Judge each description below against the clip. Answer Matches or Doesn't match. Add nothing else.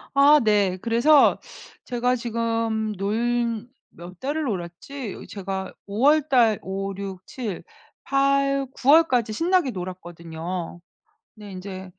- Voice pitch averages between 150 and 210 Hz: Doesn't match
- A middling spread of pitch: Doesn't match